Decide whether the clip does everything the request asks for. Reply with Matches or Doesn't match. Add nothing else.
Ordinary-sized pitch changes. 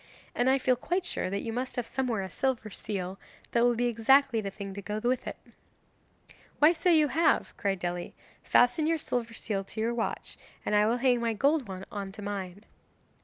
Matches